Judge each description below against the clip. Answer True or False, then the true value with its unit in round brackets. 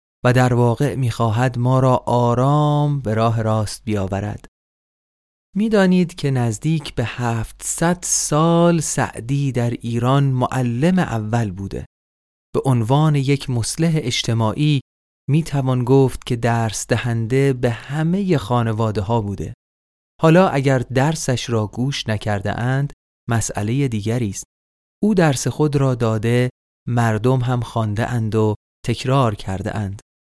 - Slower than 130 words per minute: True (120 wpm)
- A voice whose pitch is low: True (120 Hz)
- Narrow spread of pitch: False (4.0 semitones)